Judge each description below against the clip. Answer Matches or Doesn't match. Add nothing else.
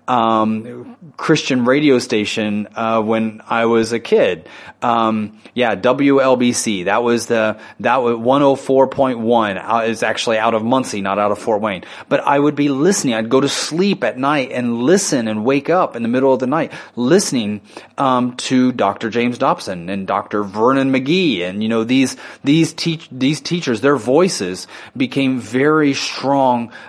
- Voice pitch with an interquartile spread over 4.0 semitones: Doesn't match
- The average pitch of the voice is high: Doesn't match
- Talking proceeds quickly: Doesn't match